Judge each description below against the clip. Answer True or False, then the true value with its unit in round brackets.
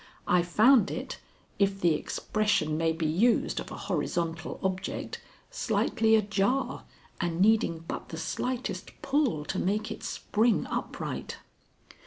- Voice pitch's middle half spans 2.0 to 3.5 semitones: False (4.8 semitones)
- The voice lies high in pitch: True (195 Hz)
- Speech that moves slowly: True (130 wpm)